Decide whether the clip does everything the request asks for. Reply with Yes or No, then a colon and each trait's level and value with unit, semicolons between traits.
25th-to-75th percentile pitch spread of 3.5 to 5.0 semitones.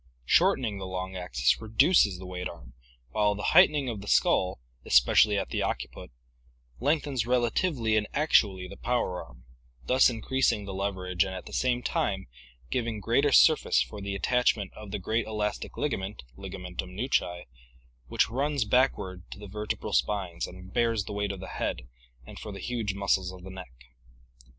Yes: average, 4.3 semitones